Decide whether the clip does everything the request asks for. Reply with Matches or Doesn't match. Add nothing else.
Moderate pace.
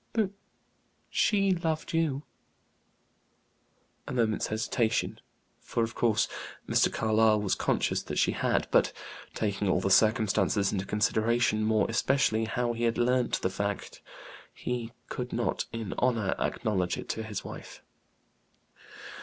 Doesn't match